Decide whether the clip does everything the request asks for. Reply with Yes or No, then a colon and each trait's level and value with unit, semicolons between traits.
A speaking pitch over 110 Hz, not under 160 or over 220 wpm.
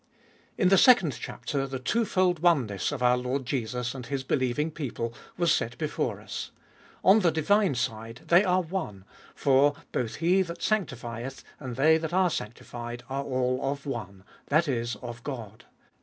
Yes: low, 135 Hz; average, 165 wpm